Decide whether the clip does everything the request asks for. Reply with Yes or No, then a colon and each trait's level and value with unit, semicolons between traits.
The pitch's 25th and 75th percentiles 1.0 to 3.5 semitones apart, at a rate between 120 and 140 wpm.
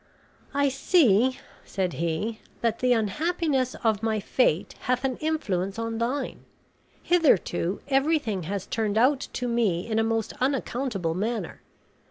No: average, 4.8 semitones; slow, 135 wpm